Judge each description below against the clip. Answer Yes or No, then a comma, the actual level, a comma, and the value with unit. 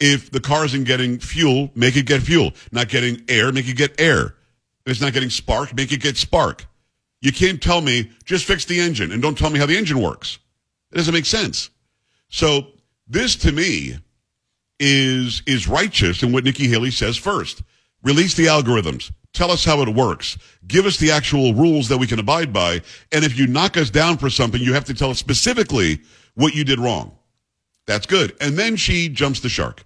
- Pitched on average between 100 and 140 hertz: Yes, low, 135 Hz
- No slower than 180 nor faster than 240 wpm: Yes, fast, 205 wpm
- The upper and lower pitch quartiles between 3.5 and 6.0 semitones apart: Yes, average, 3.8 semitones